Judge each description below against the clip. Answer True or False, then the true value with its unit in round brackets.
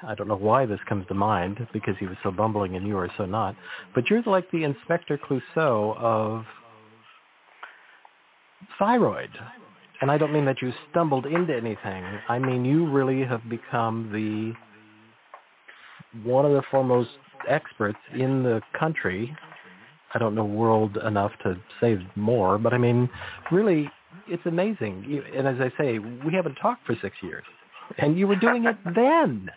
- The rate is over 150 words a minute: True (160 wpm)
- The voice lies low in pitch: True (120 Hz)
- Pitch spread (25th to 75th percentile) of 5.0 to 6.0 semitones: True (5.3 semitones)